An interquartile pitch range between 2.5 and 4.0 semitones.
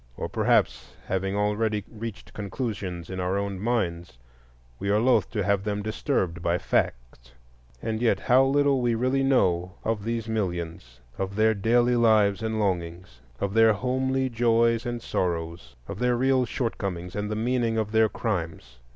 No: average, 4.4 semitones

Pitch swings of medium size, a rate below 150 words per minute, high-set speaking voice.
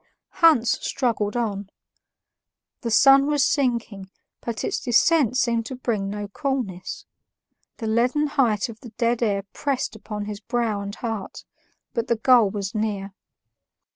Yes: average, 3.5 semitones; average, 140 wpm; high, 230 Hz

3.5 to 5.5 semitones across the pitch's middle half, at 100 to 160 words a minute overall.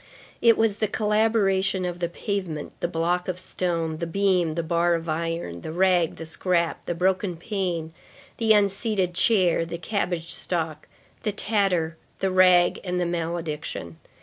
No: average, 2.7 semitones; average, 155 wpm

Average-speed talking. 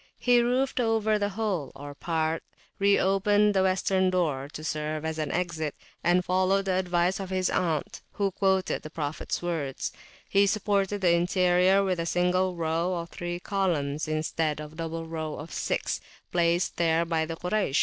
Yes: average, 180 wpm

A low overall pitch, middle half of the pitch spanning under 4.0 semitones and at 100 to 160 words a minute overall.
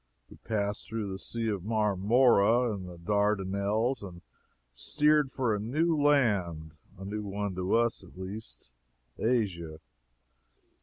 Yes: low, 105 Hz; average, 3.6 semitones; slow, 135 wpm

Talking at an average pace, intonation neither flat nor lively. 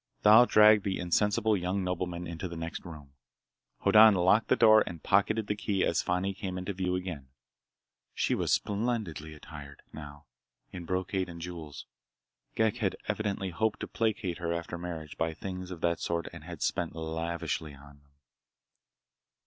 Yes: average, 165 wpm; average, 3.4 semitones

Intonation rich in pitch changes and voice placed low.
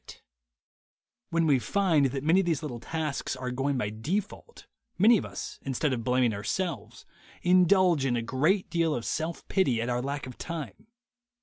No: wide, 5.8 semitones; medium, 145 Hz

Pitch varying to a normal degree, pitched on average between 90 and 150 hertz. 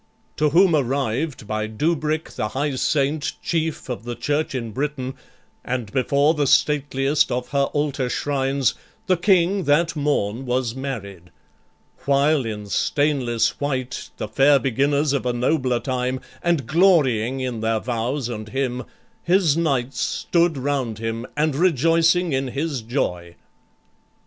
Yes: average, 3.6 semitones; low, 135 Hz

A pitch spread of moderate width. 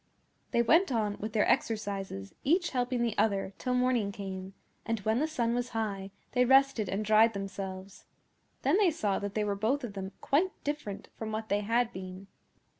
Yes: average, 4.0 semitones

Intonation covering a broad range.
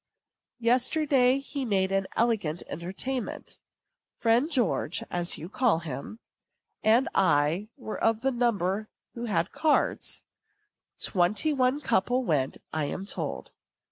Yes: wide, 6.1 semitones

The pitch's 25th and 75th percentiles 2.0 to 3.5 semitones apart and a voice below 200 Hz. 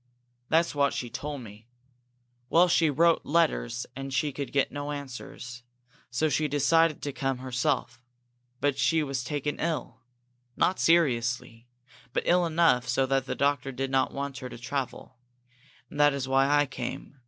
Yes: average, 2.7 semitones; medium, 140 Hz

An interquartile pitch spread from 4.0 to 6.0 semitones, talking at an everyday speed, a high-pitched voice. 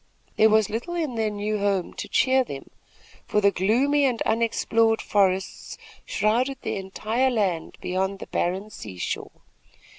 No: average, 3.5 semitones; average, 145 wpm; high, 215 Hz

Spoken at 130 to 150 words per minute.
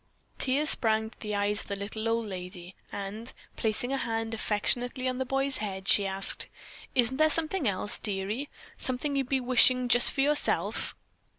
No: average, 175 wpm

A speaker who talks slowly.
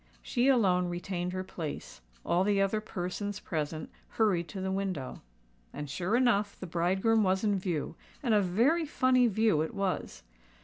No: average, 165 wpm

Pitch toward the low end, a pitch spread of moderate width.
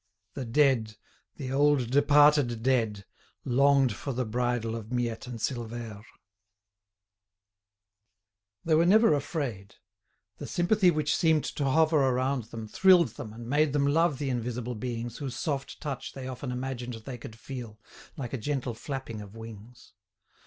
Yes: low, 130 Hz; average, 3.8 semitones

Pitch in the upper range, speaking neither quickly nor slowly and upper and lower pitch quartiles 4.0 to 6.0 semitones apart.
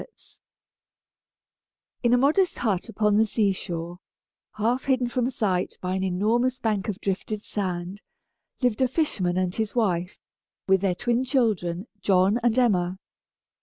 Yes: high, 210 Hz; average, 145 wpm; average, 4.6 semitones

